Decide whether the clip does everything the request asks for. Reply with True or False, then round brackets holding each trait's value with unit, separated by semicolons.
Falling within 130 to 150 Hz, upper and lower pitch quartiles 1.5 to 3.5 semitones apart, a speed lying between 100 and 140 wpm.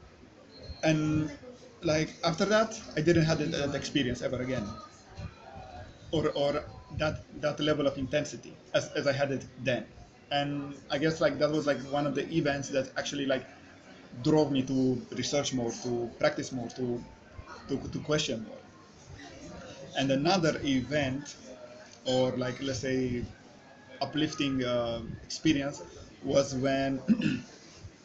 True (140 Hz; 2.8 semitones; 135 wpm)